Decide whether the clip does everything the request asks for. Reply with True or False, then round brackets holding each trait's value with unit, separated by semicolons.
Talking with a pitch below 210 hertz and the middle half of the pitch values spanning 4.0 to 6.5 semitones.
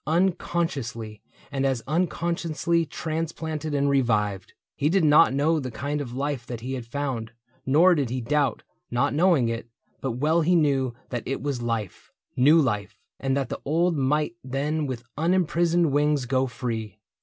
True (140 Hz; 4.4 semitones)